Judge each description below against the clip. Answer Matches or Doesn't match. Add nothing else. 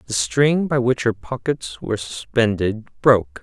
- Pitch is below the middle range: Matches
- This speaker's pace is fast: Doesn't match